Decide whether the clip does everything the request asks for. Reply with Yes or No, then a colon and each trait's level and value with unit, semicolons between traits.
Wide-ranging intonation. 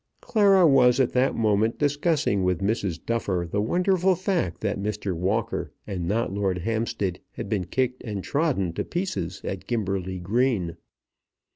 Yes: wide, 5.8 semitones